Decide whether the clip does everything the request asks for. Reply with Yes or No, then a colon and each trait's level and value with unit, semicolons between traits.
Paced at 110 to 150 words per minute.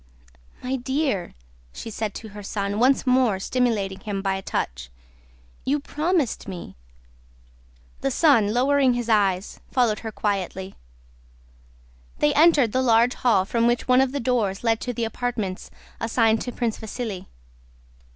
Yes: average, 145 wpm